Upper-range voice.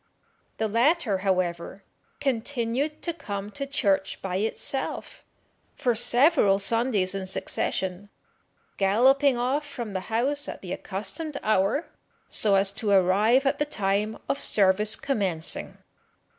Yes: high, 215 Hz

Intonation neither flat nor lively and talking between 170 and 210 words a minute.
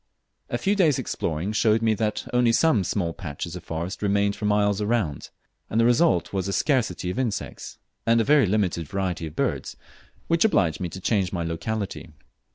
Yes: average, 4.5 semitones; average, 185 wpm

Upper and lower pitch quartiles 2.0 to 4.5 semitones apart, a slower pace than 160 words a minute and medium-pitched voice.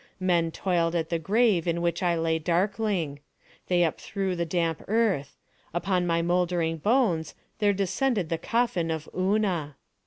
Yes: average, 3.1 semitones; average, 150 wpm; medium, 175 Hz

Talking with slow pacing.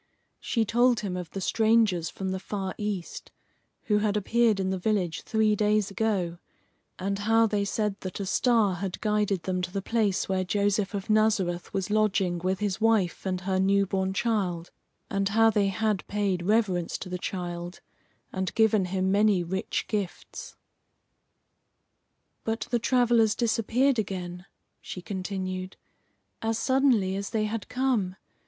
No: average, 155 wpm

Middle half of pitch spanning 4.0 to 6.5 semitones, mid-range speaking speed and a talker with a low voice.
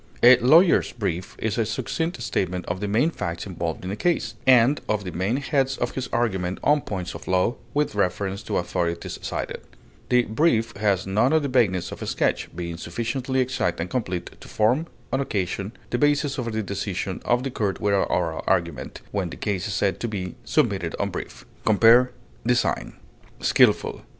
Yes: average, 5.2 semitones; average, 185 wpm; low, 110 Hz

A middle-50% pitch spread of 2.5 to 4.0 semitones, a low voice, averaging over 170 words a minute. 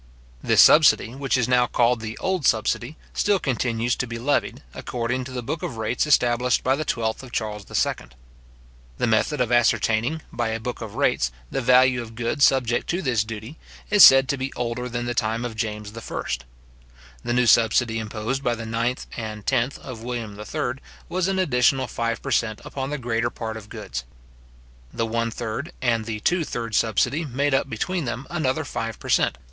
Yes: average, 2.9 semitones; low, 120 Hz; average, 195 wpm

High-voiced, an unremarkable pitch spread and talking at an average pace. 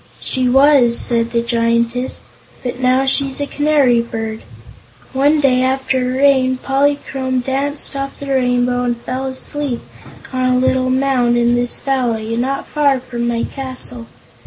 No: very high, 255 Hz; narrow, 2.0 semitones; average, 150 wpm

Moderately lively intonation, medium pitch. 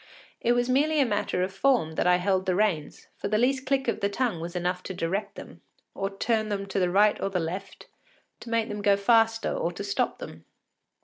No: average, 4.0 semitones; high, 205 Hz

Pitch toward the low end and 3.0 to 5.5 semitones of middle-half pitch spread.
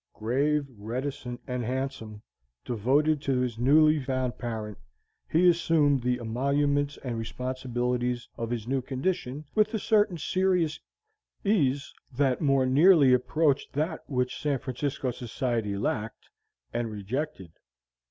Yes: low, 130 Hz; average, 3.4 semitones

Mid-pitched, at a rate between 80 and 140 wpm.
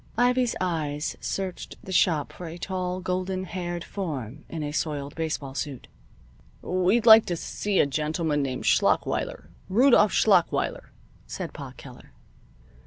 Yes: medium, 175 Hz; slow, 135 wpm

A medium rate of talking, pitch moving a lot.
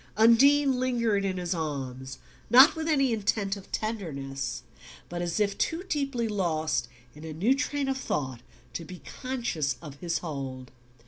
Yes: average, 155 wpm; wide, 8.8 semitones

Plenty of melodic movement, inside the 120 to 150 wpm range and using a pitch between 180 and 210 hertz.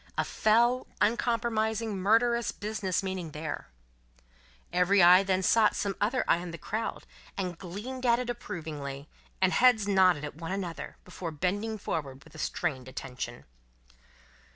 No: average, 4.9 semitones; average, 145 wpm; high, 190 Hz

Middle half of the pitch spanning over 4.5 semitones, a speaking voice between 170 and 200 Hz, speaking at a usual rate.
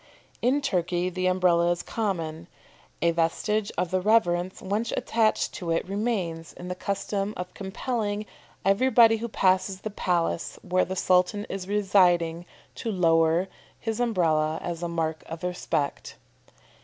No: average, 3.4 semitones; medium, 185 Hz; average, 145 wpm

